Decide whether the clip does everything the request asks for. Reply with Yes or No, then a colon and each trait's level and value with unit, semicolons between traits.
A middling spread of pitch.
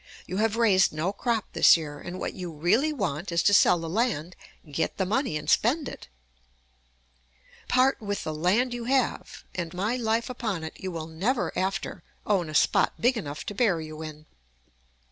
No: wide, 6.2 semitones